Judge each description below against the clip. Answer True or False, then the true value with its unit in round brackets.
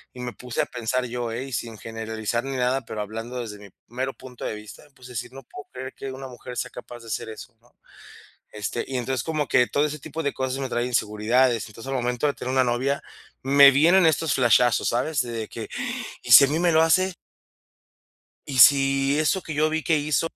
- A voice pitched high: False (130 Hz)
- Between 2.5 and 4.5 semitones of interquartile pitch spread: True (2.9 semitones)